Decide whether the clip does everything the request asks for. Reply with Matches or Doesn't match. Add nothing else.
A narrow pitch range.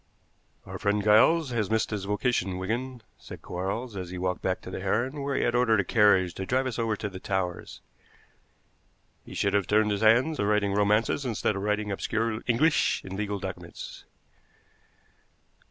Doesn't match